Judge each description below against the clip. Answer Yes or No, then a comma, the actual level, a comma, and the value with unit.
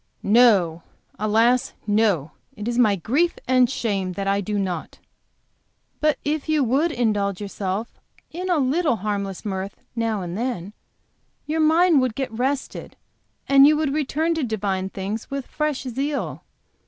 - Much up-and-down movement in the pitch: Yes, wide, 6.1 semitones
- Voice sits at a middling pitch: No, high, 230 Hz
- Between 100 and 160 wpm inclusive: Yes, average, 150 wpm